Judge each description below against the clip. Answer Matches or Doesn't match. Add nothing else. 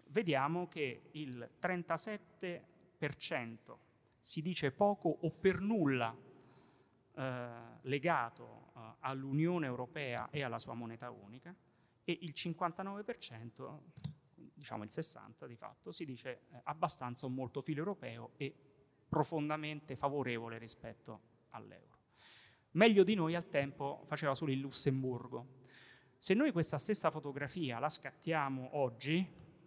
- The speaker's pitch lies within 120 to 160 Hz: Matches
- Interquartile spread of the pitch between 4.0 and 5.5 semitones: Matches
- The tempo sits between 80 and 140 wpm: Matches